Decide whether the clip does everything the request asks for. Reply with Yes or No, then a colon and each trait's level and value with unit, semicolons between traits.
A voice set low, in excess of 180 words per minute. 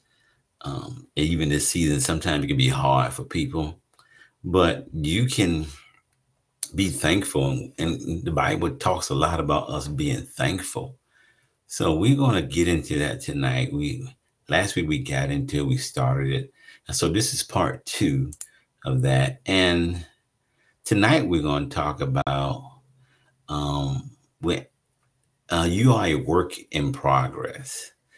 No: low, 115 Hz; average, 145 wpm